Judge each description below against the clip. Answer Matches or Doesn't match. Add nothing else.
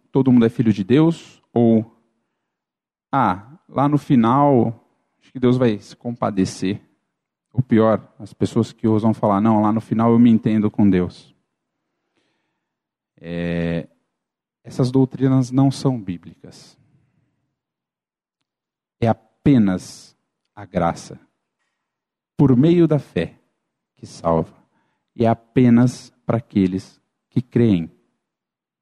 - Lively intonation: Doesn't match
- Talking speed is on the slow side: Matches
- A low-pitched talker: Matches